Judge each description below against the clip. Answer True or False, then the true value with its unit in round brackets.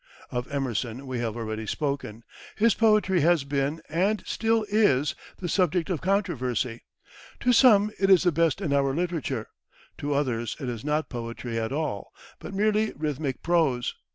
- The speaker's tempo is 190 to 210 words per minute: False (160 wpm)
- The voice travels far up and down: True (7.0 semitones)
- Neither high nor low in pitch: True (150 Hz)